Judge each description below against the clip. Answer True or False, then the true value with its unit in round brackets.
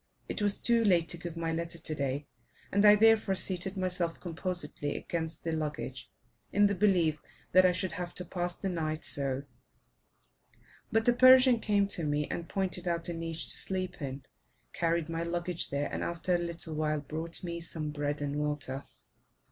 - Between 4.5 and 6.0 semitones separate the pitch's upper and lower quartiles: False (3.1 semitones)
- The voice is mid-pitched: True (170 Hz)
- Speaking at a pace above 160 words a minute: True (180 wpm)